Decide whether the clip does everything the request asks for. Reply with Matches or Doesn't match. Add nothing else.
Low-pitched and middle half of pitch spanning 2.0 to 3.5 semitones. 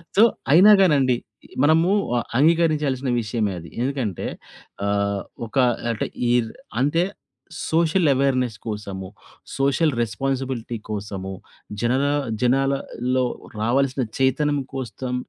Doesn't match